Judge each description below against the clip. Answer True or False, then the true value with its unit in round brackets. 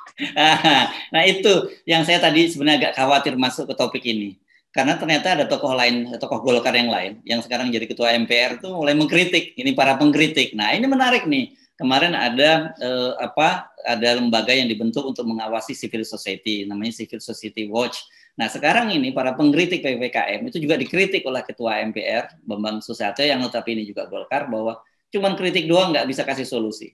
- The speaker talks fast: True (180 wpm)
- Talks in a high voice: False (125 Hz)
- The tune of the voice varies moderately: False (6.1 semitones)